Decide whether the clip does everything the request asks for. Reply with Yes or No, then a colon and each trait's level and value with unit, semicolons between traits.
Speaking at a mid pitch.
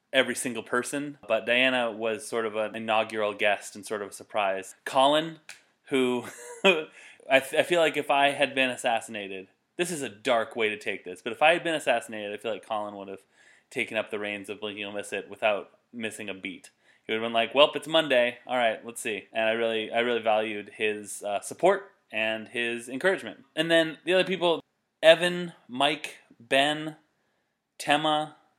No: low, 120 Hz